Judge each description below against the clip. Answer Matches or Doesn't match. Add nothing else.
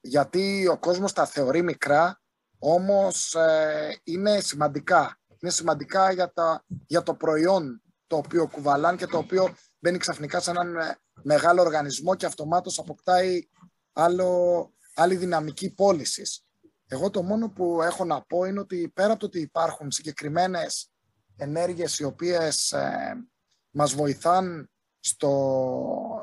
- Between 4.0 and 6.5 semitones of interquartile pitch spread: Doesn't match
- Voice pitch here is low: Doesn't match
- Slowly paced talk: Doesn't match